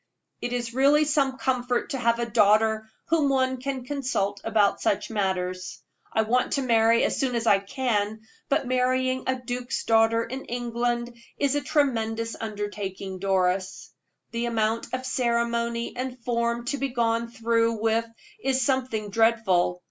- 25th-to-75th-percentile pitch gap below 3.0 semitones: Yes, narrow, 2.6 semitones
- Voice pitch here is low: No, high, 235 Hz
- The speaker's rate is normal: Yes, average, 155 wpm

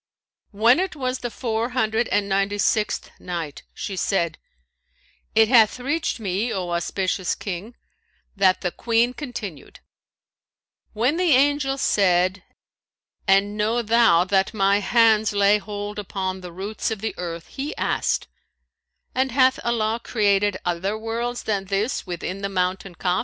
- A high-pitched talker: Yes, high, 210 Hz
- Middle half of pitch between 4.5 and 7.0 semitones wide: No, average, 3.7 semitones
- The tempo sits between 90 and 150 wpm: Yes, average, 140 wpm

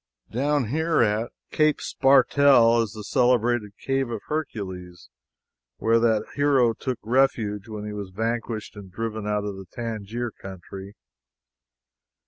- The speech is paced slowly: Yes, slow, 130 wpm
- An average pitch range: Yes, average, 3.5 semitones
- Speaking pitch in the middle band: No, low, 115 Hz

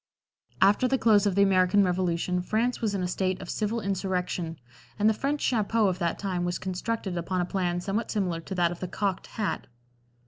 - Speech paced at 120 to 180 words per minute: No, fast, 205 wpm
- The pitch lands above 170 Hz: Yes, high, 190 Hz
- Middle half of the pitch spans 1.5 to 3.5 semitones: Yes, average, 2.9 semitones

